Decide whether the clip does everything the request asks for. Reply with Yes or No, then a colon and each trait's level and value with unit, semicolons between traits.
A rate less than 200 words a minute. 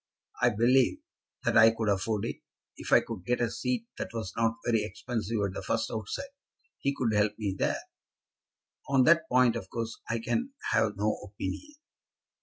Yes: average, 180 wpm